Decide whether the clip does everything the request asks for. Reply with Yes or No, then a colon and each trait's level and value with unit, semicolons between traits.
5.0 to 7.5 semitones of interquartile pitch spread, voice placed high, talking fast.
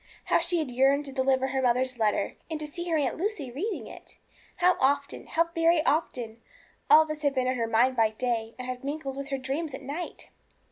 No: average, 3.7 semitones; very high, 275 Hz; fast, 220 wpm